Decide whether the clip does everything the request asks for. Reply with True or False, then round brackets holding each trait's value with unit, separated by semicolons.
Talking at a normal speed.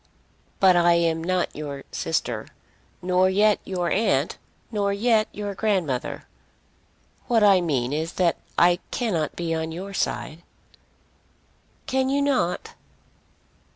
False (120 wpm)